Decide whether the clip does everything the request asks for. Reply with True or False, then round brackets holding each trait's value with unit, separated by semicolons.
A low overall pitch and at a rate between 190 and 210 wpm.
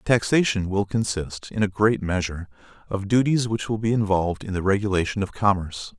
False (100 Hz; 180 wpm)